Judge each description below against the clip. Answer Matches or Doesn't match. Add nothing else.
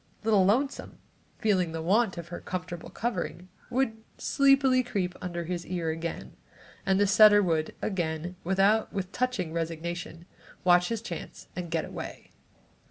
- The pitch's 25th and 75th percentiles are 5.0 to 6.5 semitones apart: Doesn't match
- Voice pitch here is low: Doesn't match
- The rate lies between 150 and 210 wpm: Doesn't match